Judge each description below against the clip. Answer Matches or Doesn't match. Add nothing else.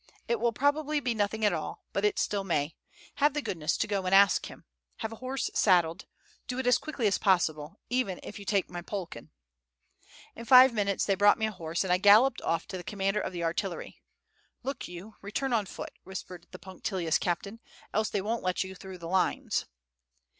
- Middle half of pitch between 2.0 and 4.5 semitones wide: Matches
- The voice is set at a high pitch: Matches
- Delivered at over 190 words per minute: Matches